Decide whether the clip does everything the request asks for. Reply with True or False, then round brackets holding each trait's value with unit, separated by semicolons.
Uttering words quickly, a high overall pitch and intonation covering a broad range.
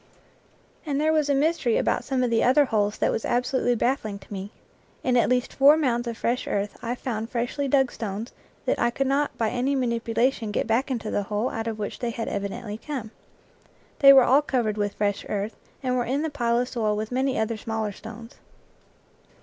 False (210 wpm; 240 Hz; 3.3 semitones)